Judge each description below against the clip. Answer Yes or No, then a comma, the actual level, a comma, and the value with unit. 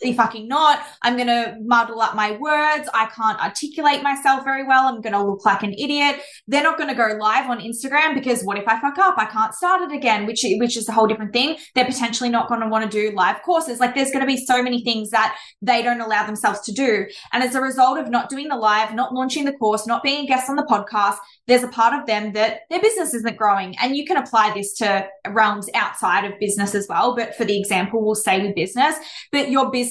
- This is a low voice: No, high, 235 Hz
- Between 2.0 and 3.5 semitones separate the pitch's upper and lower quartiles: No, average, 4.0 semitones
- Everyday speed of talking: No, fast, 255 wpm